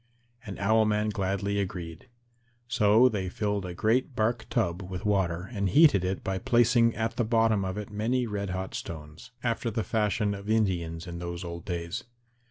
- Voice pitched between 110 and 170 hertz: No, low, 100 Hz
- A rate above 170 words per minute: Yes, average, 180 wpm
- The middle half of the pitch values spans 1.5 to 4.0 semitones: Yes, average, 3.4 semitones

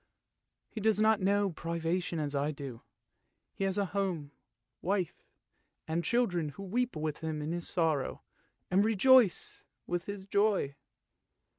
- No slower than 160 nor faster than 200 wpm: No, average, 140 wpm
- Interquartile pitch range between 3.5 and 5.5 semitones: Yes, average, 4.3 semitones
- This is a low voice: No, medium, 180 Hz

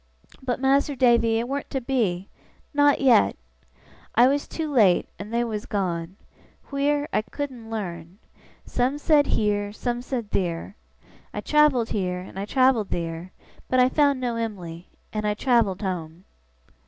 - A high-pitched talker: Yes, high, 230 Hz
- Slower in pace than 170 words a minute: Yes, average, 155 wpm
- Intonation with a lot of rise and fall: Yes, wide, 5.7 semitones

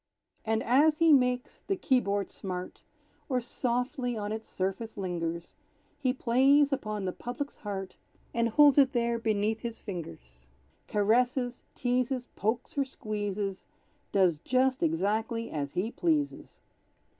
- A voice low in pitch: No, high, 230 Hz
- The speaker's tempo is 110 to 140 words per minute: Yes, slow, 135 wpm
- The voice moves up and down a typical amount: Yes, average, 4.3 semitones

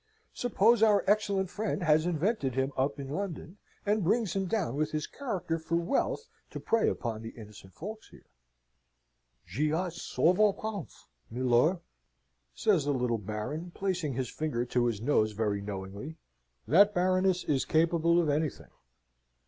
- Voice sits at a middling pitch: Yes, medium, 160 Hz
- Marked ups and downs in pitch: Yes, wide, 7.1 semitones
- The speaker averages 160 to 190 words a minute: No, average, 150 wpm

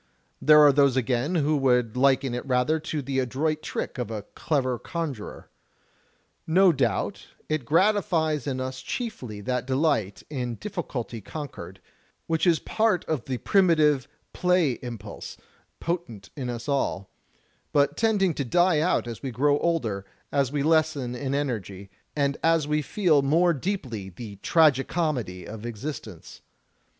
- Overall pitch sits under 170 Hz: Yes, medium, 140 Hz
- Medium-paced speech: Yes, average, 150 wpm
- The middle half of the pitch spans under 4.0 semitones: No, average, 4.6 semitones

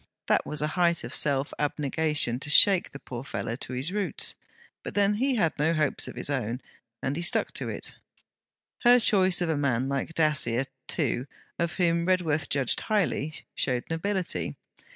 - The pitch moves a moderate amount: Yes, average, 4.5 semitones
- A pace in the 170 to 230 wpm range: Yes, average, 175 wpm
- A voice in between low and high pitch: Yes, medium, 155 Hz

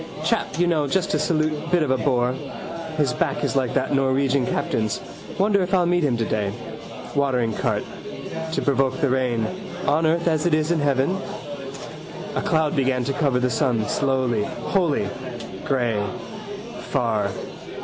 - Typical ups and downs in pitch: Yes, average, 4.0 semitones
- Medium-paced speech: Yes, average, 160 wpm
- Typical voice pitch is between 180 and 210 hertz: No, medium, 140 Hz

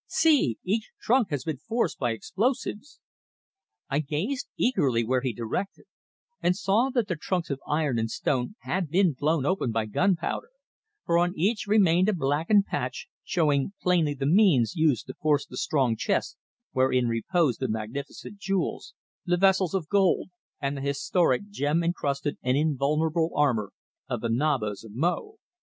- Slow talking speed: No, average, 160 wpm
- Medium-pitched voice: Yes, medium, 155 Hz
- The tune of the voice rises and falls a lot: Yes, wide, 6.2 semitones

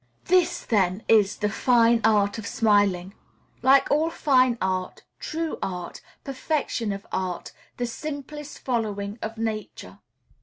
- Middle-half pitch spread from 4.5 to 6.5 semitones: Yes, average, 4.8 semitones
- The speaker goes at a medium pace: No, slow, 125 wpm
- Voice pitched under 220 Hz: No, high, 225 Hz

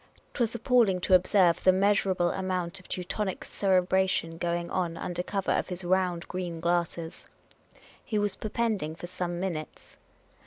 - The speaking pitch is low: No, medium, 185 Hz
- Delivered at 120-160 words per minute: Yes, average, 155 wpm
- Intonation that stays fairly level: Yes, narrow, 2.0 semitones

